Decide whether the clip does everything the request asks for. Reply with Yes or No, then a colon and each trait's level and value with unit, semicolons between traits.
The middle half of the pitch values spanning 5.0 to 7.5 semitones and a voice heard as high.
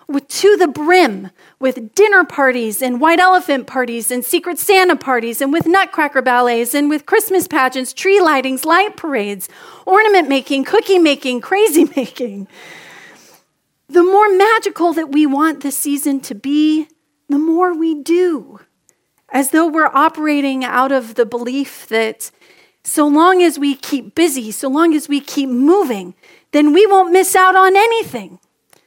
Yes: wide, 5.4 semitones; very high, 300 Hz